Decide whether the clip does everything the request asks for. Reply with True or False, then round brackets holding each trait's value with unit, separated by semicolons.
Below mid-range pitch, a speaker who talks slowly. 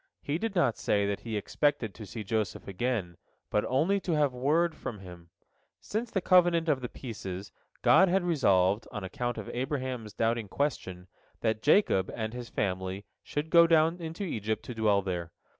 False (120 Hz; 175 wpm)